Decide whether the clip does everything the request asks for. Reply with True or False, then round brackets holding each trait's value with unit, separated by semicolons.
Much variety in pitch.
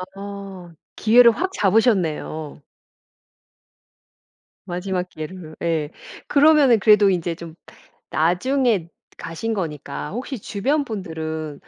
True (5.7 semitones)